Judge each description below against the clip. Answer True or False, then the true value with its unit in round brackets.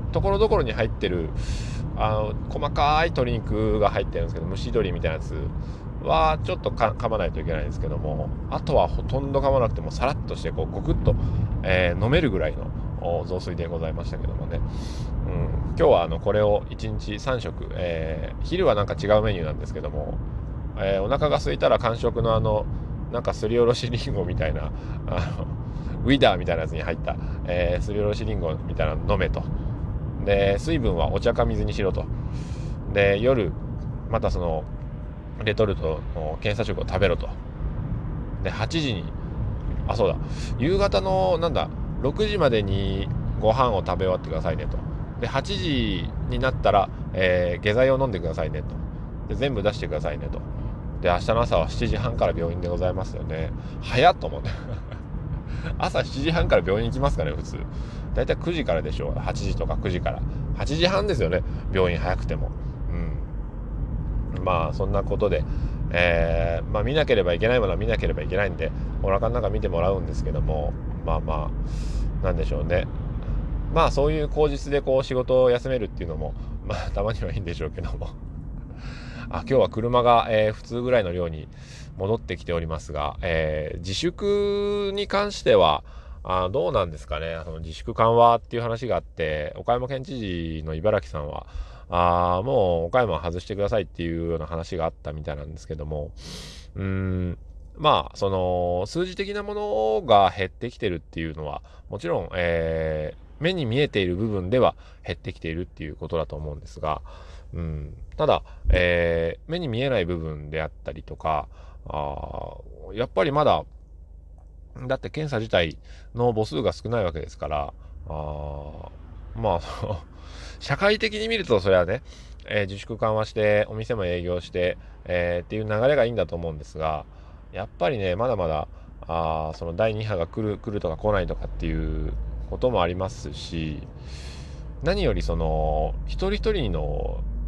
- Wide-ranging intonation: True (6.3 semitones)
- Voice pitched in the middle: False (90 Hz)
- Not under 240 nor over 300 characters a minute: False (340 characters per minute)